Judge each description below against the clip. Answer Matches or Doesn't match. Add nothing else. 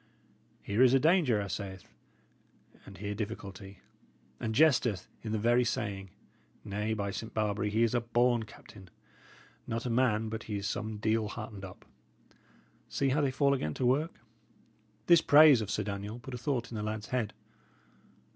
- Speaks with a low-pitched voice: Matches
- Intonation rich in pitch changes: Doesn't match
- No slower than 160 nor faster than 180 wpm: Matches